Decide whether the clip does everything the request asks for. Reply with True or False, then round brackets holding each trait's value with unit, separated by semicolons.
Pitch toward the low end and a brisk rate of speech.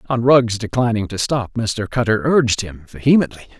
False (115 Hz; 165 wpm)